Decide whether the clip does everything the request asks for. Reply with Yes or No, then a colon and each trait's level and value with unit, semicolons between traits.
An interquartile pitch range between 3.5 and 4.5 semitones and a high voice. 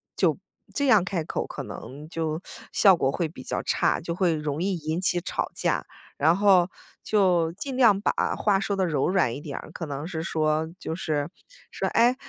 No: average, 3.9 semitones; medium, 170 Hz